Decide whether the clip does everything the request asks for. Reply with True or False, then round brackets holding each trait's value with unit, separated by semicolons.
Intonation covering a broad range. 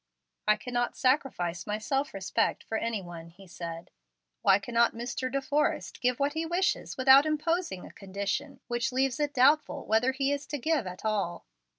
True (5.9 semitones)